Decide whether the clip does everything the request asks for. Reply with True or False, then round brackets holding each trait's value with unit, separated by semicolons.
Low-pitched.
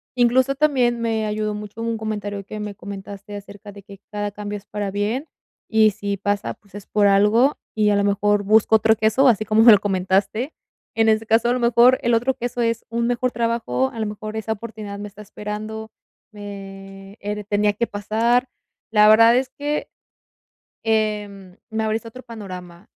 False (215 Hz)